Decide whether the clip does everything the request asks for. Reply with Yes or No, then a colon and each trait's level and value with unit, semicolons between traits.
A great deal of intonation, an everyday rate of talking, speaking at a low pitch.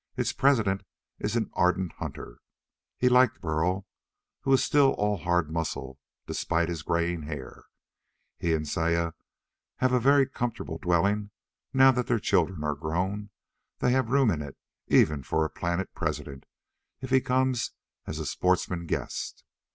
Yes: wide, 7.3 semitones; average, 155 wpm; very low, 90 Hz